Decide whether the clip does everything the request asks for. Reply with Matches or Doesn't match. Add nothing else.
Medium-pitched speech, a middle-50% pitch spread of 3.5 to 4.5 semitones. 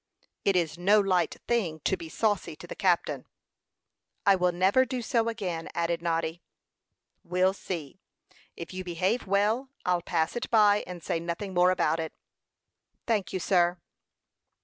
Doesn't match